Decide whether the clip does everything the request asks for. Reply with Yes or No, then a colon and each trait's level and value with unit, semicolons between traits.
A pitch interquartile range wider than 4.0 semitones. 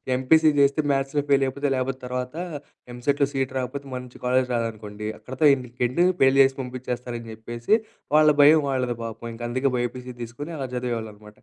No: narrow, 2.4 semitones